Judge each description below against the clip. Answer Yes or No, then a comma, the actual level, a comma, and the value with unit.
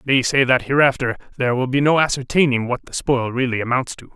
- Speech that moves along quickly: Yes, fast, 215 wpm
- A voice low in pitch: Yes, low, 130 Hz